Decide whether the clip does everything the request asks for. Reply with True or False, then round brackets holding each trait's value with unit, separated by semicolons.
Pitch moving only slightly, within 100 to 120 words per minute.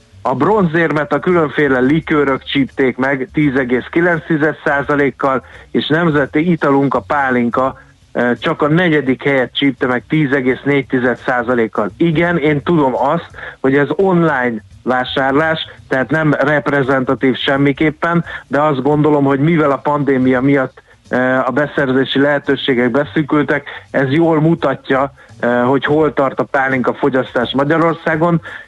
False (3.0 semitones; 115 wpm)